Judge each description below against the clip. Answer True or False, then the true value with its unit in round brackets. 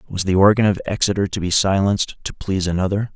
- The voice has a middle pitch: False (95 Hz)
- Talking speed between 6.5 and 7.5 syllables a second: True (6.7 syllables/s)